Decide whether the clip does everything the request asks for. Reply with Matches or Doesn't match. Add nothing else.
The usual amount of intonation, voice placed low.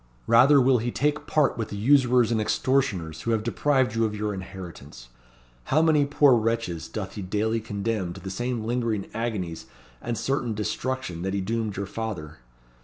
Matches